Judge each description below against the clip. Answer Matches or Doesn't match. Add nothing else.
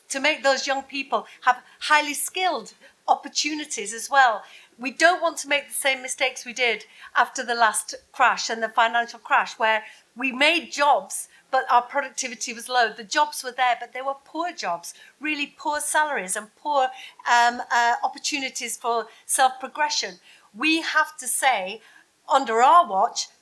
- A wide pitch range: Doesn't match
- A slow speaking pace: Doesn't match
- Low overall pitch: Doesn't match